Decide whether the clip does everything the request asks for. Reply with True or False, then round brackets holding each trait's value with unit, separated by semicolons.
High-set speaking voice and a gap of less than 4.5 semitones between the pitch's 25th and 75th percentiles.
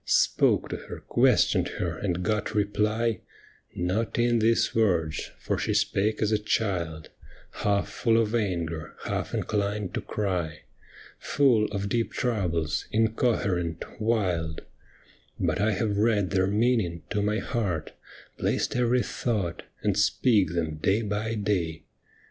False (105 Hz; 4.0 semitones)